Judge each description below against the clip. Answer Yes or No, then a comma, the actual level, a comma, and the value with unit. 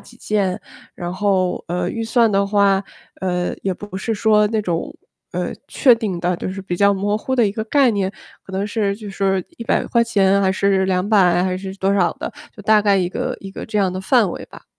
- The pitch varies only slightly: Yes, narrow, 2.1 semitones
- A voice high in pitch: Yes, high, 200 Hz